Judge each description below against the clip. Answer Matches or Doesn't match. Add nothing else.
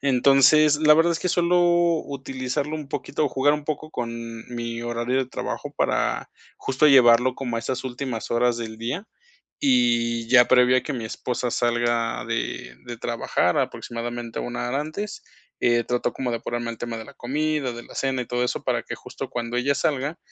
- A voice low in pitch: Matches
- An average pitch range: Matches